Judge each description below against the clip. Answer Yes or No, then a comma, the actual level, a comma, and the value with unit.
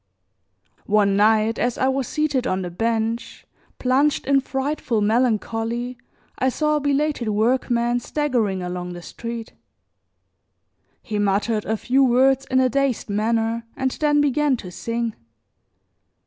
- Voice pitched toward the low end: No, high, 235 Hz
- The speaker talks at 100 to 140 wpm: Yes, slow, 135 wpm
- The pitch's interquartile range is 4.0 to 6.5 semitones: No, average, 3.5 semitones